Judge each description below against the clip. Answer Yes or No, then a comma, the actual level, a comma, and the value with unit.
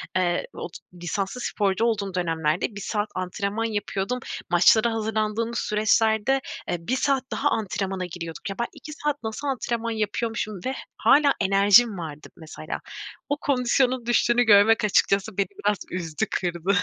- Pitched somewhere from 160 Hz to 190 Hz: No, high, 210 Hz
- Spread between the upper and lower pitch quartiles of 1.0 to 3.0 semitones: No, average, 3.9 semitones